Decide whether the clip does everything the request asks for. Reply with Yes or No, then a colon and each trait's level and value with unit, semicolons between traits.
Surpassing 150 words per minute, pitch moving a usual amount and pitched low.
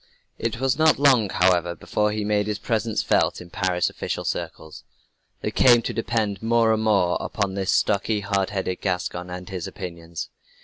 Yes: average, 175 wpm; average, 3.6 semitones; low, 100 Hz